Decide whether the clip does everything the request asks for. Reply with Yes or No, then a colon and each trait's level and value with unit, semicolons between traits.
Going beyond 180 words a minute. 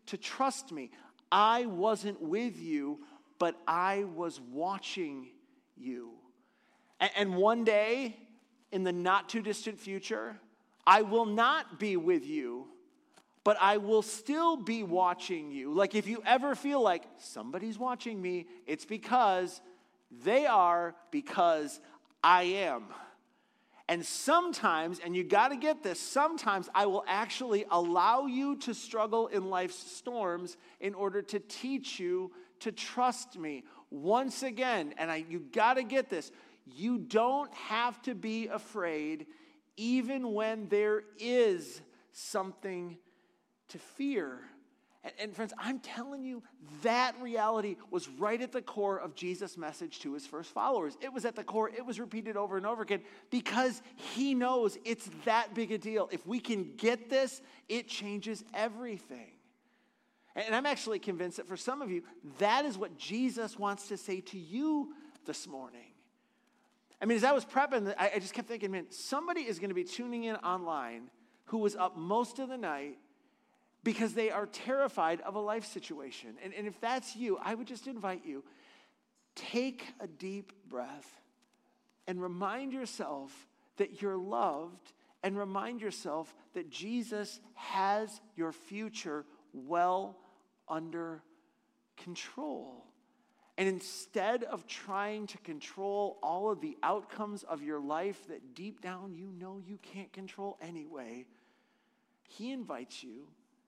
No: average, 145 wpm